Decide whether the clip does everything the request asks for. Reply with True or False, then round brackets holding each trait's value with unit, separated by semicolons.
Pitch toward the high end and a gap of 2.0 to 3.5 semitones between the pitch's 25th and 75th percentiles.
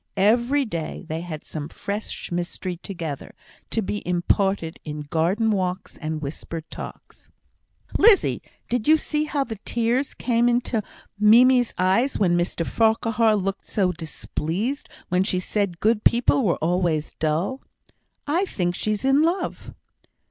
False (200 Hz; 5.5 semitones)